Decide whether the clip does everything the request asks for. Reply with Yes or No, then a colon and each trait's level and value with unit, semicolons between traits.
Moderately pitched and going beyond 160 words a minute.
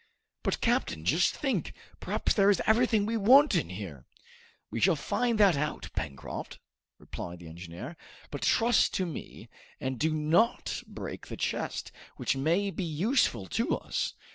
No: medium, 165 Hz; average, 155 wpm